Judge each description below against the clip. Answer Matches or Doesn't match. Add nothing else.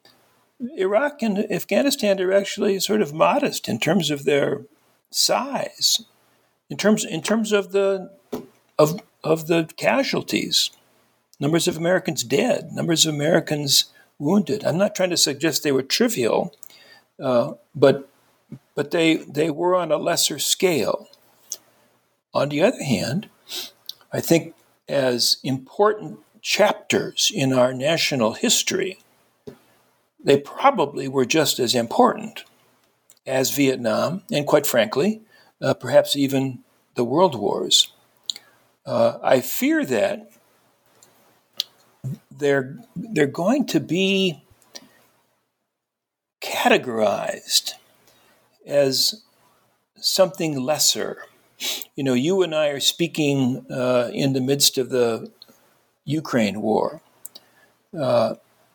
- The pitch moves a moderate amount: Doesn't match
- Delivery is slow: Matches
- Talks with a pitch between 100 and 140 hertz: Doesn't match